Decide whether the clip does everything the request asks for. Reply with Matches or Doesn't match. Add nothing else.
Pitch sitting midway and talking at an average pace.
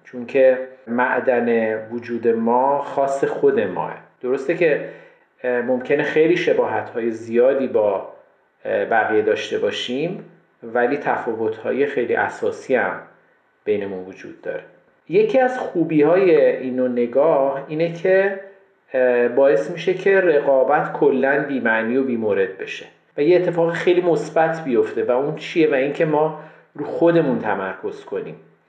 Matches